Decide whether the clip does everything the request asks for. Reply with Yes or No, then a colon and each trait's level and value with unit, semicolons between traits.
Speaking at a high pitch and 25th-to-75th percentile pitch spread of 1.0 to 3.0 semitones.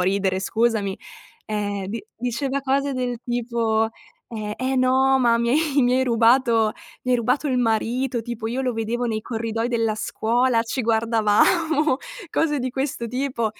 Yes: high, 235 Hz; average, 2.7 semitones